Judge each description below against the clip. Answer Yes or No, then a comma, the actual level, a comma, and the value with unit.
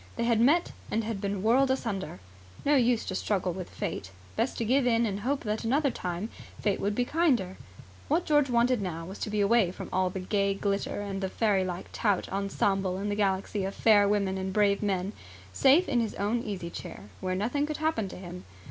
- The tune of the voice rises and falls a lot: No, average, 3.8 semitones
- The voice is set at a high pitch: Yes, high, 205 Hz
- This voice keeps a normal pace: No, fast, 210 wpm